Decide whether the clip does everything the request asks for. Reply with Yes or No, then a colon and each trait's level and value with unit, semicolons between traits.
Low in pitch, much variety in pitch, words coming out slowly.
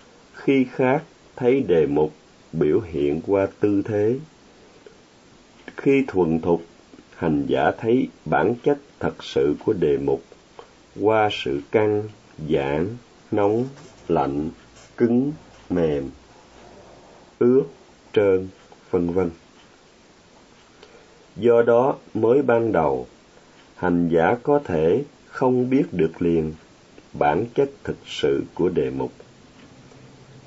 Yes: low, 105 Hz; wide, 7.3 semitones; slow, 110 wpm